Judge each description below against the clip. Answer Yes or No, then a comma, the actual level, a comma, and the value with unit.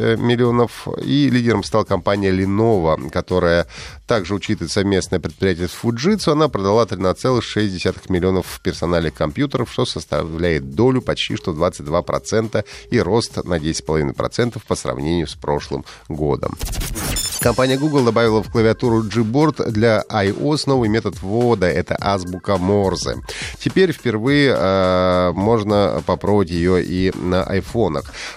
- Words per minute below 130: Yes, average, 120 wpm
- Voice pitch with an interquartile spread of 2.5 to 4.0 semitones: No, average, 4.5 semitones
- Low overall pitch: Yes, low, 100 Hz